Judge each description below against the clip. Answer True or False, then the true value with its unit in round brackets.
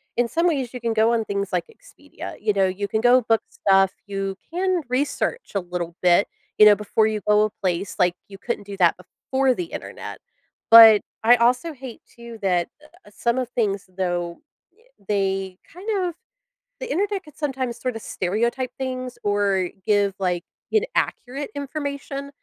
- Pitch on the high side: True (225 Hz)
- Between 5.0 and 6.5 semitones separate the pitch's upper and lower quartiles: True (5.3 semitones)